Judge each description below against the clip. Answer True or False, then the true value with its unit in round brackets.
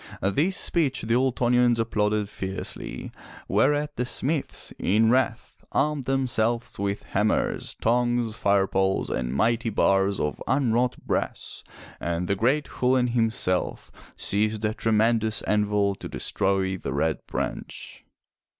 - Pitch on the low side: True (110 Hz)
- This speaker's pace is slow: True (125 wpm)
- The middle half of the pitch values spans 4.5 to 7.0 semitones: False (3.7 semitones)